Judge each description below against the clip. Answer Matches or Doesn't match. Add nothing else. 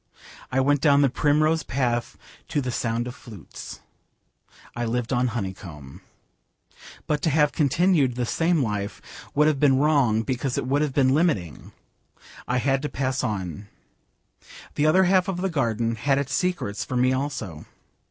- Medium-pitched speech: Doesn't match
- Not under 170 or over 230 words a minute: Doesn't match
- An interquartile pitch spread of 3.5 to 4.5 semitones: Matches